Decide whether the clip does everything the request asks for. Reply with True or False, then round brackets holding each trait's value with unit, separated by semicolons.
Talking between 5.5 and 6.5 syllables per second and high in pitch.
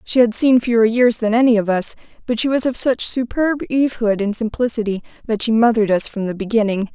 True (5.9 syllables/s; 225 Hz)